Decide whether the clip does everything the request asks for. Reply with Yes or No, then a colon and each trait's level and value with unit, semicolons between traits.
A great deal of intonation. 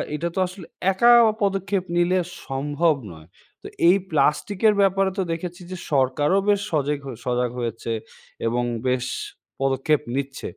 Yes: wide, 5.8 semitones